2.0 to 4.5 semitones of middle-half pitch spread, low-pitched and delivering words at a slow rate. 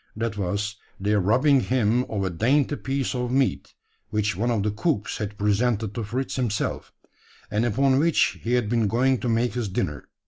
No: average, 3.5 semitones; low, 115 Hz; average, 185 wpm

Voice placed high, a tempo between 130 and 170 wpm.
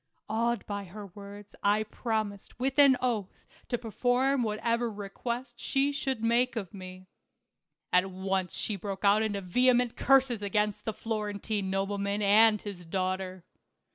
Yes: high, 210 Hz; average, 160 wpm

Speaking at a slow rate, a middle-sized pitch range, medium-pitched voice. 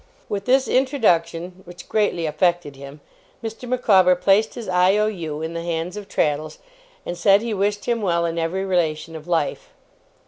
No: average, 165 wpm; average, 4.0 semitones; medium, 180 Hz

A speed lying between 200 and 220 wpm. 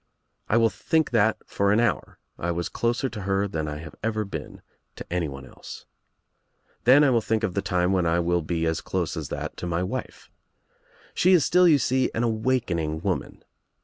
Yes: fast, 205 wpm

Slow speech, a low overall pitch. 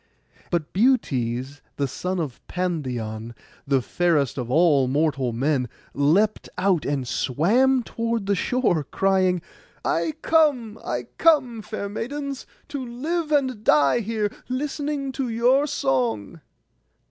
No: slow, 125 wpm; high, 190 Hz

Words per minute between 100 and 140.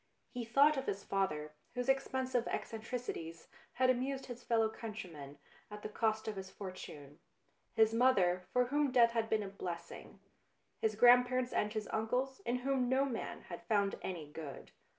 No: average, 170 wpm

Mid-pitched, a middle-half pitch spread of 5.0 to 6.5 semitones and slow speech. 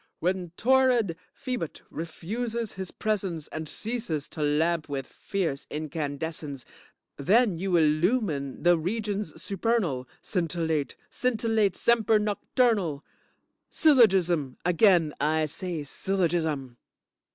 Yes: medium, 175 Hz; wide, 5.6 semitones; slow, 95 wpm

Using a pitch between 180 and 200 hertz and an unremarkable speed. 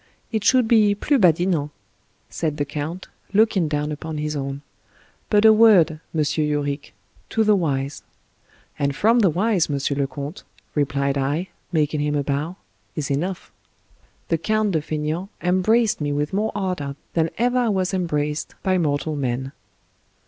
No: medium, 160 Hz; average, 170 wpm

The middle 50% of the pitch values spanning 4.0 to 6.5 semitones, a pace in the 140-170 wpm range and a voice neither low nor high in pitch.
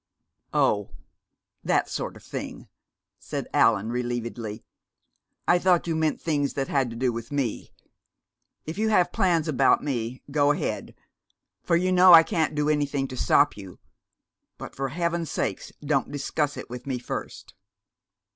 Yes: average, 5.0 semitones; average, 155 wpm; medium, 145 Hz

